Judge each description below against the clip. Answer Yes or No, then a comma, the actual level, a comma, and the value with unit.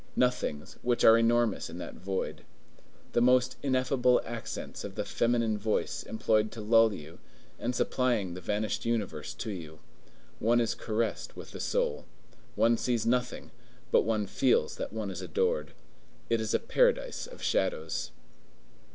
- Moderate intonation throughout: Yes, average, 3.2 semitones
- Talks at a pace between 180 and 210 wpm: No, average, 150 wpm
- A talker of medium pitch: No, low, 110 Hz